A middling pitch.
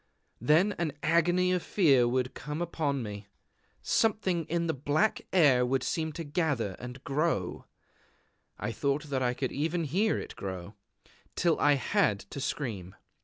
Yes: medium, 145 Hz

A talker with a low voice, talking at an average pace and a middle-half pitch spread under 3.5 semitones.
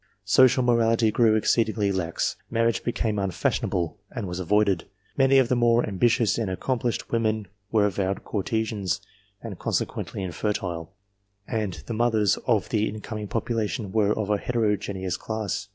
Yes: low, 110 Hz; average, 145 wpm; average, 2.8 semitones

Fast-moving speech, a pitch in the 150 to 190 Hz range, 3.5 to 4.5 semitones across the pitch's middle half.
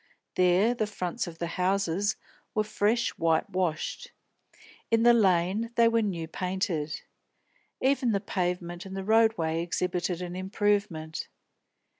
No: slow, 135 wpm; medium, 185 Hz; average, 3.8 semitones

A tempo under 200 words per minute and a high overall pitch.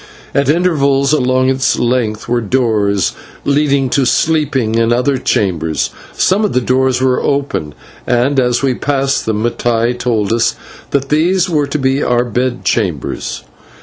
No: average, 150 wpm; low, 130 Hz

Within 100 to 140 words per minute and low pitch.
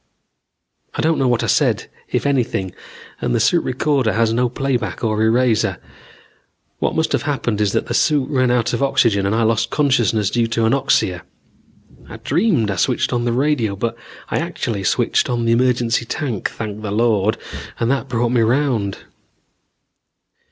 No: average, 175 wpm; low, 120 Hz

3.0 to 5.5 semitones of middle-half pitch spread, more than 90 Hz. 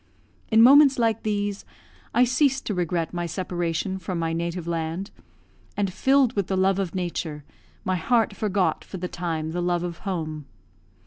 Yes: average, 3.7 semitones; medium, 185 Hz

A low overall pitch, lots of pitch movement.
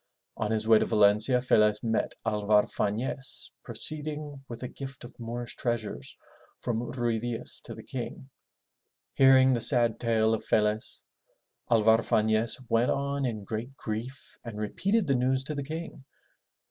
No: low, 120 Hz; average, 3.3 semitones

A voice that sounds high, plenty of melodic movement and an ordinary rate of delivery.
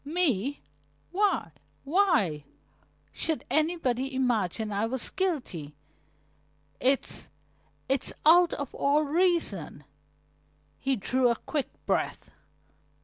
No: very high, 270 Hz; wide, 6.3 semitones; slow, 90 wpm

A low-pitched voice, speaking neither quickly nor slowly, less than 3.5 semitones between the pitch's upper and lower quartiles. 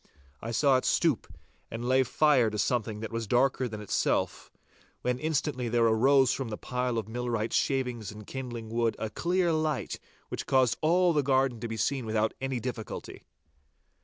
Yes: low, 125 Hz; average, 175 wpm; average, 3.1 semitones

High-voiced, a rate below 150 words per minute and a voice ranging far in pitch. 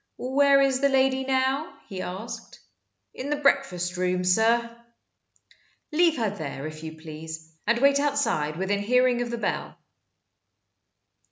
Yes: high, 235 Hz; average, 140 wpm; wide, 7.1 semitones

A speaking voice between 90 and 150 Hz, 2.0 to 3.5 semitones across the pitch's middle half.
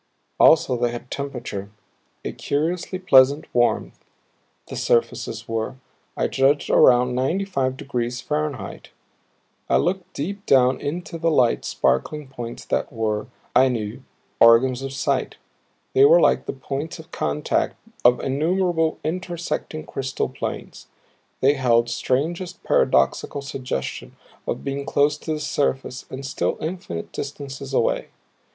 No: low, 135 Hz; average, 4.2 semitones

